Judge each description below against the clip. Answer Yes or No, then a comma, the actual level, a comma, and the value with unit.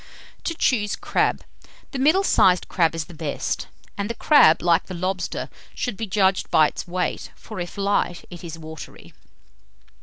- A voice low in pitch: No, medium, 185 Hz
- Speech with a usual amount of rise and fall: Yes, average, 3.7 semitones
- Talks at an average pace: Yes, average, 170 wpm